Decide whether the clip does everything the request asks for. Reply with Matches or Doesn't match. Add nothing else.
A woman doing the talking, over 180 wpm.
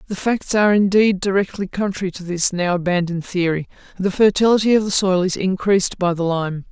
Matches